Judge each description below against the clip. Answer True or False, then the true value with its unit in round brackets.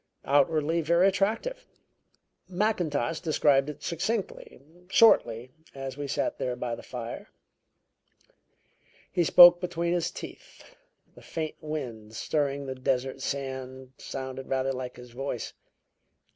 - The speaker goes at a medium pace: False (115 wpm)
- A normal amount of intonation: True (4.7 semitones)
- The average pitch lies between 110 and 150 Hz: True (140 Hz)